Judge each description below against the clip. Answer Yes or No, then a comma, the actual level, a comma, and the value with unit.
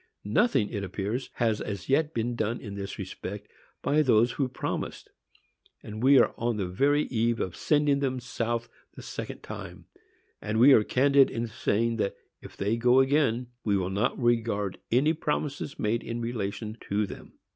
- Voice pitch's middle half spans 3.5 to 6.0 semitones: Yes, average, 3.9 semitones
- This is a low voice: Yes, low, 115 Hz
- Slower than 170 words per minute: No, average, 175 wpm